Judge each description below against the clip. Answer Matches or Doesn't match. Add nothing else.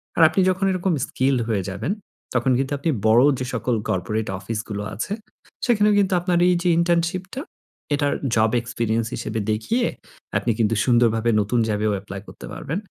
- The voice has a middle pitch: Doesn't match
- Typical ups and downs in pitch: Doesn't match